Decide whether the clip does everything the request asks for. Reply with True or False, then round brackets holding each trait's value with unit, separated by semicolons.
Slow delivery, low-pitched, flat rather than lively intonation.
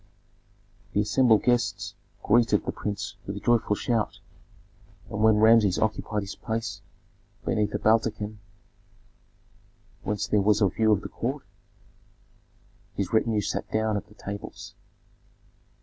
True (130 wpm; 105 Hz; 1.6 semitones)